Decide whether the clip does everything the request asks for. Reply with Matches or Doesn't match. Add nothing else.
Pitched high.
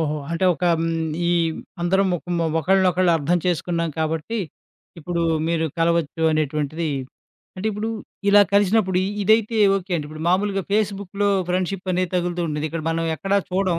Doesn't match